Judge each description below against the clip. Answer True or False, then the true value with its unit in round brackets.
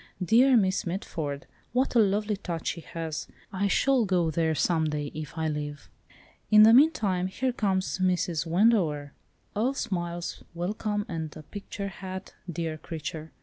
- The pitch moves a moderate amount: True (4.5 semitones)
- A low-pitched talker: False (180 Hz)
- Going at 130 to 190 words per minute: True (150 wpm)